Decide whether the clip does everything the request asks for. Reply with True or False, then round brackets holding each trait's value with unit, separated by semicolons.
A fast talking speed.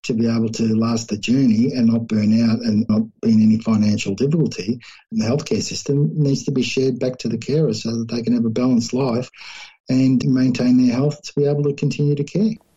True (230 wpm)